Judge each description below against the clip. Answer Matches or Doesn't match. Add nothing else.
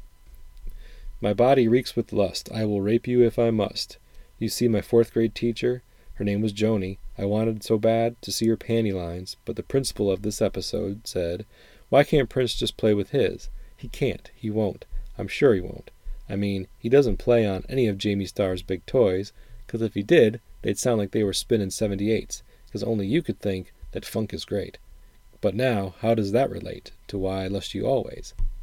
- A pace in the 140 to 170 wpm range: Doesn't match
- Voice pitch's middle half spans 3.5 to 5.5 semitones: Doesn't match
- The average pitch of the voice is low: Matches